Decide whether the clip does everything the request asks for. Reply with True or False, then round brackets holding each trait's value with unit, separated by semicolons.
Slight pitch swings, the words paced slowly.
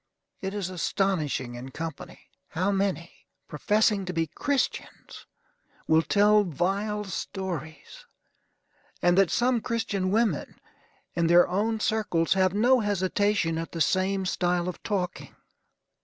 False (3.6 semitones; 125 wpm)